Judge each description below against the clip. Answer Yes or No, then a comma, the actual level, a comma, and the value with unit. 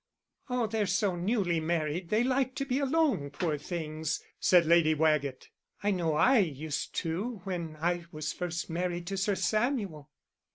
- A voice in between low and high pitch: Yes, medium, 175 Hz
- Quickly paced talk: No, average, 160 wpm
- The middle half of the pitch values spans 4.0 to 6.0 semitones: Yes, average, 5.2 semitones